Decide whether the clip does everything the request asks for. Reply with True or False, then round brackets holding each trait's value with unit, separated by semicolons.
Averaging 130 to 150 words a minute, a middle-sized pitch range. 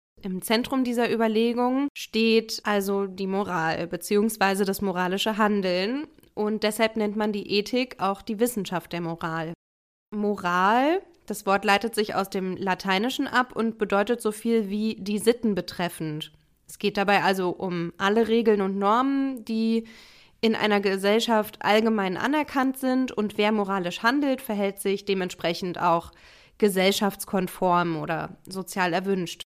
True (140 wpm; 3.1 semitones)